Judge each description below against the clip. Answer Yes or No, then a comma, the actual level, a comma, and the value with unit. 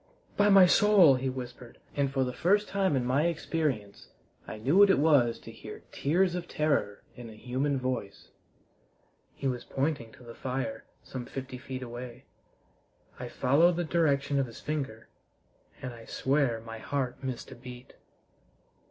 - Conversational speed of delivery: Yes, average, 165 wpm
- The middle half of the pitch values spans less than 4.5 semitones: Yes, average, 4.1 semitones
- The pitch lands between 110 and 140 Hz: Yes, low, 135 Hz